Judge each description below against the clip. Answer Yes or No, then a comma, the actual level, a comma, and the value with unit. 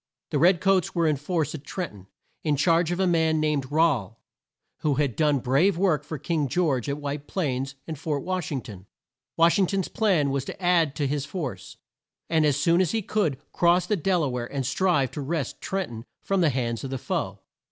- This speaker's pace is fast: Yes, fast, 220 wpm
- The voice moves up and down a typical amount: Yes, average, 4.3 semitones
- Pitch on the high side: No, medium, 155 Hz